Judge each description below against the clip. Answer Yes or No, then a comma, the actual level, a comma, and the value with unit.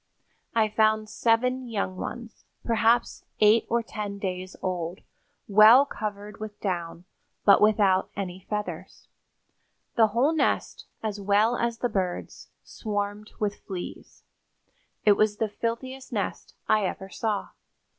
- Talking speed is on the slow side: Yes, slow, 125 wpm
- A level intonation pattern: Yes, narrow, 2.3 semitones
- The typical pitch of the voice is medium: No, high, 210 Hz